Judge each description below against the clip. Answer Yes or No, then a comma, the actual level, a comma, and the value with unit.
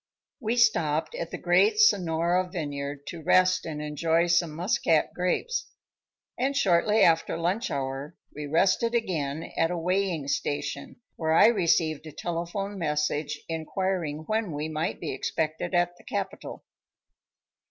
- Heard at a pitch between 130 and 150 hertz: No, medium, 170 Hz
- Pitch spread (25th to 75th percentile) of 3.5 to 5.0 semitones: Yes, average, 3.8 semitones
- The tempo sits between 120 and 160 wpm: Yes, average, 140 wpm